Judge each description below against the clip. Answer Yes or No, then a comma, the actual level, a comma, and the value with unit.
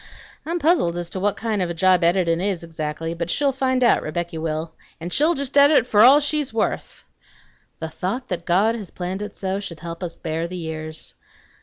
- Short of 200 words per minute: No, fast, 205 wpm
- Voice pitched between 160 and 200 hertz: Yes, medium, 185 Hz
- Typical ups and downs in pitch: No, wide, 6.1 semitones